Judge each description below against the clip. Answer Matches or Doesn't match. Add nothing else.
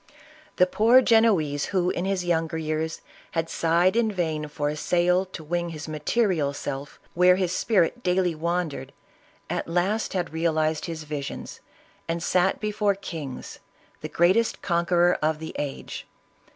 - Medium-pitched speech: Matches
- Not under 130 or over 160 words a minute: Matches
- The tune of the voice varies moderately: Matches